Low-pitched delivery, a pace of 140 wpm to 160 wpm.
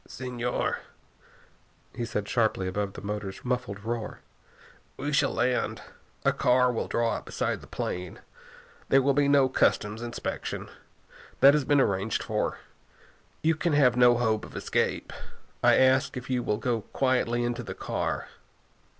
Yes: low, 120 Hz; average, 155 wpm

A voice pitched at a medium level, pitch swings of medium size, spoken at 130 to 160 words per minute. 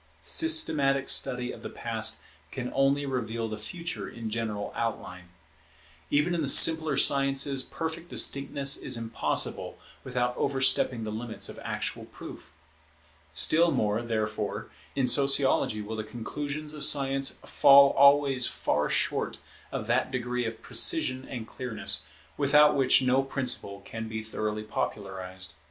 No: low, 130 Hz; average, 4.0 semitones; slow, 135 wpm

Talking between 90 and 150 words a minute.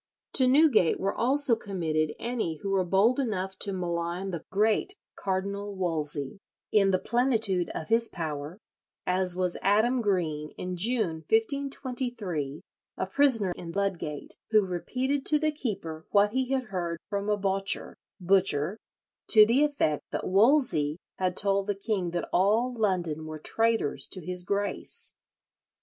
Yes: average, 145 wpm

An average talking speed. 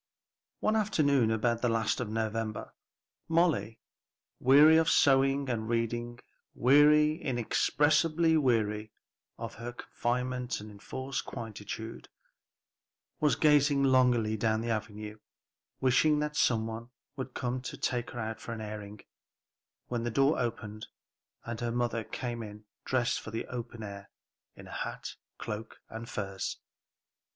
No: slow, 130 wpm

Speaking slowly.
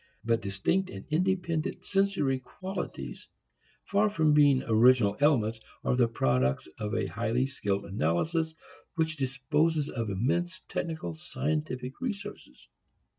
Yes: slow, 120 wpm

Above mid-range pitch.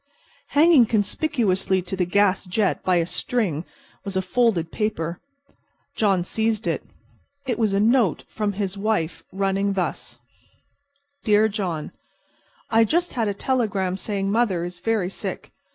Yes: high, 200 Hz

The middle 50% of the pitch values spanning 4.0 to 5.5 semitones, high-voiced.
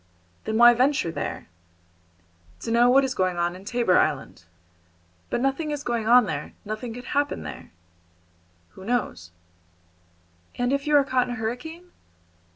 Yes: average, 5.0 semitones; high, 240 Hz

